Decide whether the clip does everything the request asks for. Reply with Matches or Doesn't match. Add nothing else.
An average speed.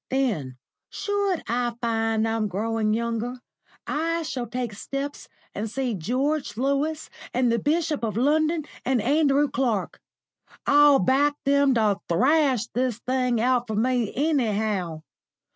Doesn't match